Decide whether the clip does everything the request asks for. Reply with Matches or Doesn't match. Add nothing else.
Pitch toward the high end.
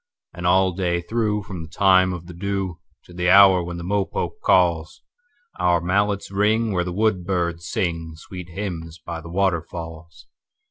Doesn't match